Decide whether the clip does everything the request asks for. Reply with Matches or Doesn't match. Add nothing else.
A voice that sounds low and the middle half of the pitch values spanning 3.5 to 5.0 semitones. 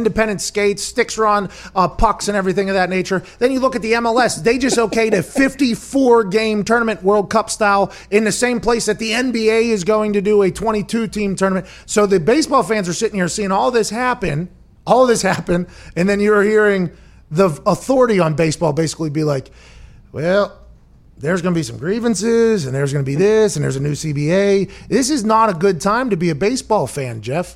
Doesn't match